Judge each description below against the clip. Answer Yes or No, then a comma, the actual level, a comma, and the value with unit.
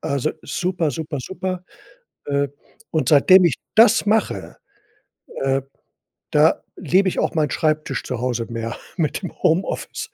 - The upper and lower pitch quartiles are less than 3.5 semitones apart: No, average, 5.3 semitones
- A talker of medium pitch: Yes, medium, 155 Hz